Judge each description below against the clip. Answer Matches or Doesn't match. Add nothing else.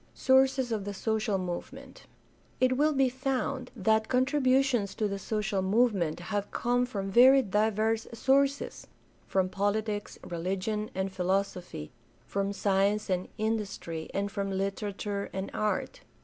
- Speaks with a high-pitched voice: Matches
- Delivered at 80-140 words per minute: Matches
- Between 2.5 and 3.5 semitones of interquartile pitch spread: Doesn't match